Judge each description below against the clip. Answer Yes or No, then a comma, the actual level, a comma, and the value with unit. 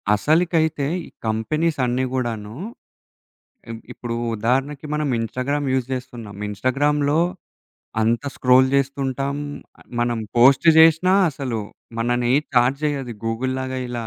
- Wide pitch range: No, average, 3.3 semitones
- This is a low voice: Yes, low, 130 Hz